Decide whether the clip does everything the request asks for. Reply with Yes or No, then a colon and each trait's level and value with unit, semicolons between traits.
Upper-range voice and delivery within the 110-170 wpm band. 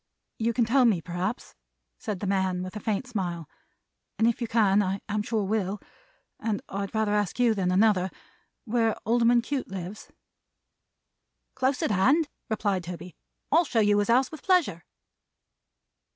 Yes: high, 210 Hz; average, 160 wpm